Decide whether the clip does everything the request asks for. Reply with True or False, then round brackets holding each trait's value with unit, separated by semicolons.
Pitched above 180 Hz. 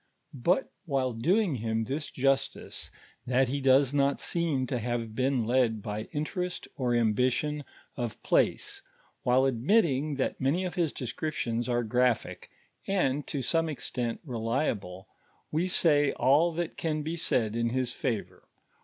False (130 Hz)